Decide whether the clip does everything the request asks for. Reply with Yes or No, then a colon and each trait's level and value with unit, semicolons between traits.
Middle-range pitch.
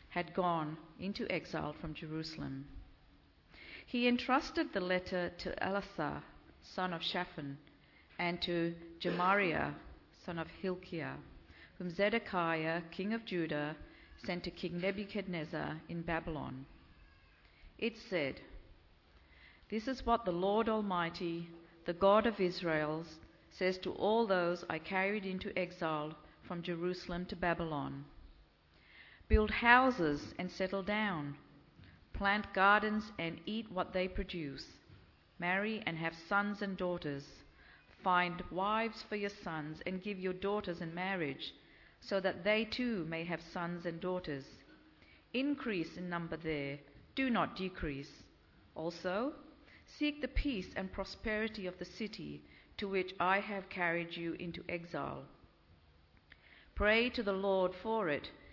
Yes: medium, 180 Hz